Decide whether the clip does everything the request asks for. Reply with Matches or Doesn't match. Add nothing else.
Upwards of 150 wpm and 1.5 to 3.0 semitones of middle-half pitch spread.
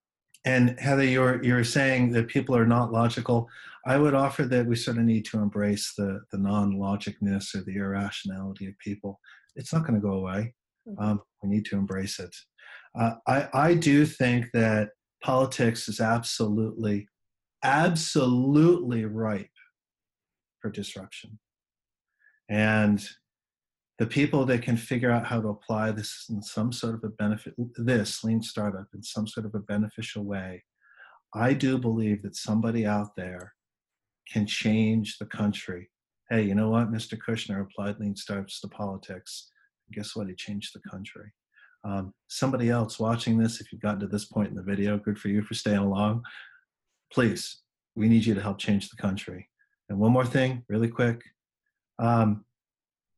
Matches